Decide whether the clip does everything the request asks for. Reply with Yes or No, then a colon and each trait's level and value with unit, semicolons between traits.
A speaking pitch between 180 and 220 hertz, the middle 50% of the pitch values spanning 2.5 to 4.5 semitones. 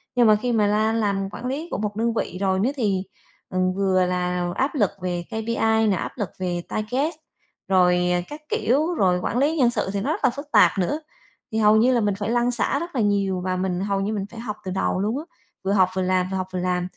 Yes: high, 205 Hz; average, 4.2 semitones